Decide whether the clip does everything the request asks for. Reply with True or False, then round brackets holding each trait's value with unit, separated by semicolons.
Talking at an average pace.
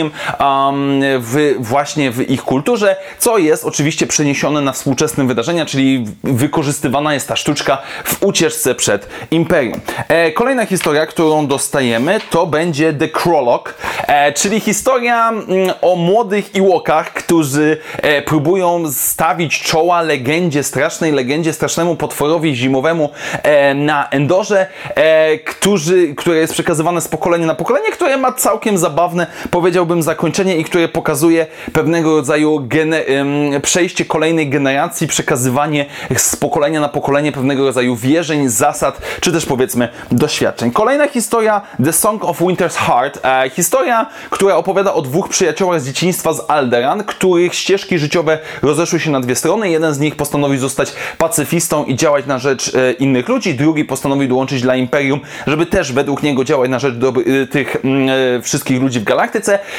True (150 wpm)